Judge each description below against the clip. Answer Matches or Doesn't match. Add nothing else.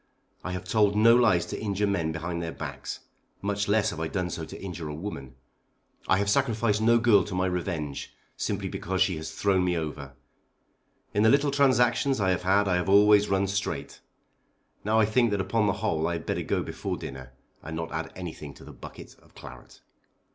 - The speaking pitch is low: Matches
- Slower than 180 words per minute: Doesn't match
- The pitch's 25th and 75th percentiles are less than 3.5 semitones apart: Doesn't match